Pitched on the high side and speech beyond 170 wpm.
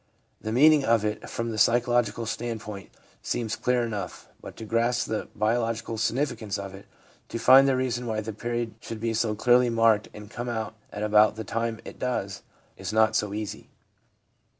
No: low, 115 Hz; average, 180 wpm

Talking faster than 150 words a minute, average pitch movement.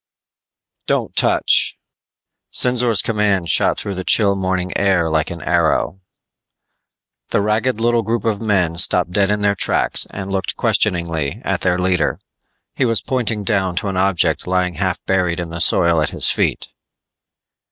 Yes: average, 160 wpm; average, 3.1 semitones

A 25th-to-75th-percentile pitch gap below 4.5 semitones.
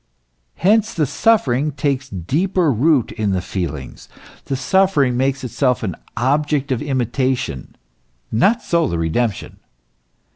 No: average, 5.2 semitones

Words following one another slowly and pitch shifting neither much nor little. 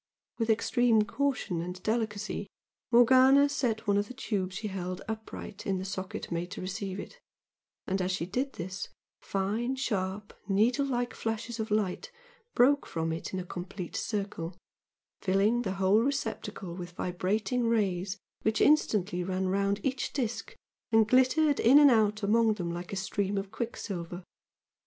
No: average, 155 wpm; average, 4.1 semitones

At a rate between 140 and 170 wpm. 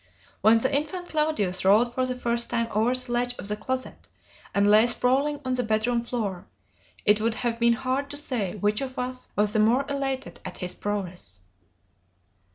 No: average, 185 wpm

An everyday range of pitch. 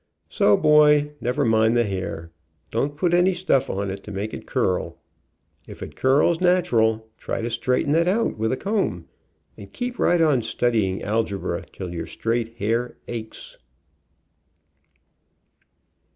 No: wide, 5.8 semitones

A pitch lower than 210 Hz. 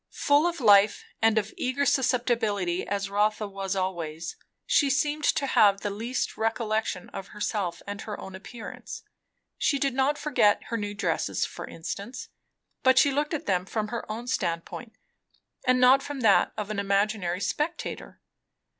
No: high, 215 Hz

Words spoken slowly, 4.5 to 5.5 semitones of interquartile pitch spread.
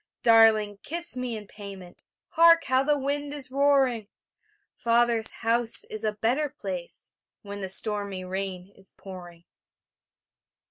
Yes: slow, 130 wpm; average, 4.9 semitones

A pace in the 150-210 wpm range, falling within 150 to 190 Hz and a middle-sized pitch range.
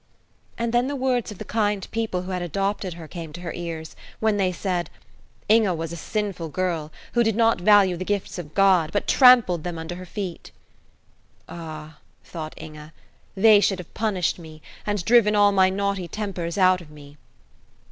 Yes: average, 185 wpm; medium, 185 Hz; average, 3.7 semitones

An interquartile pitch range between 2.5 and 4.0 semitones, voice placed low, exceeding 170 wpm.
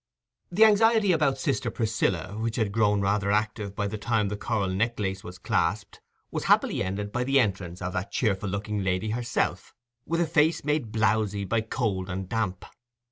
Yes: average, 3.7 semitones; low, 105 Hz; average, 180 wpm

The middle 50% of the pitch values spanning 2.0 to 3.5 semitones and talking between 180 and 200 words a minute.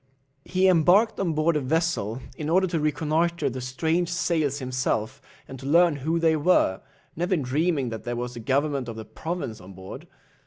No: average, 5.0 semitones; average, 185 wpm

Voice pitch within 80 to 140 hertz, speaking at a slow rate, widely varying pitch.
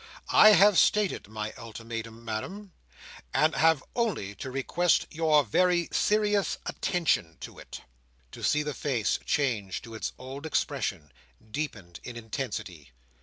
Yes: low, 135 Hz; slow, 130 wpm; wide, 7.9 semitones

